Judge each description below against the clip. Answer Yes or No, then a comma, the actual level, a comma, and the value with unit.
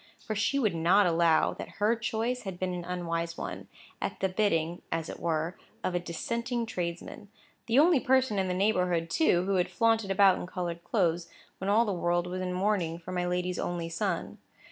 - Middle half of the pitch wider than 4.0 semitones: No, average, 3.6 semitones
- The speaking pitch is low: No, medium, 180 Hz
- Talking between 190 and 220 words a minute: Yes, average, 200 wpm